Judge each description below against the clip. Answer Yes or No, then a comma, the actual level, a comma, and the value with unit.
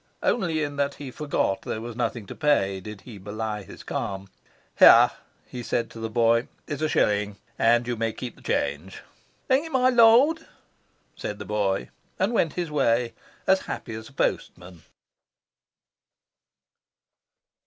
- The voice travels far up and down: Yes, wide, 6.4 semitones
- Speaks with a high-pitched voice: No, low, 120 Hz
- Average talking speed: Yes, average, 155 wpm